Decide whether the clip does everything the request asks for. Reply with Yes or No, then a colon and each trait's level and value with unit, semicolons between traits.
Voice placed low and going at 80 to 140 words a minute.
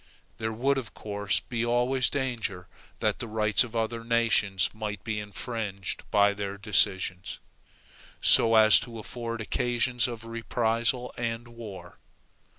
Yes: low, 115 Hz; slow, 135 wpm